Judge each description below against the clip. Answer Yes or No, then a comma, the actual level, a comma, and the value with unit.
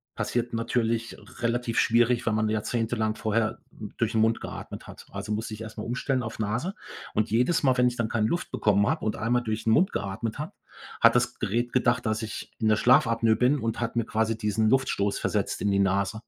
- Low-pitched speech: Yes, low, 115 Hz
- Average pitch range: No, narrow, 1.9 semitones